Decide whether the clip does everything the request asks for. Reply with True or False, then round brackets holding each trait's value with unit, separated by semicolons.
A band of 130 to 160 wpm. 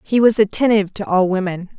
False (200 wpm)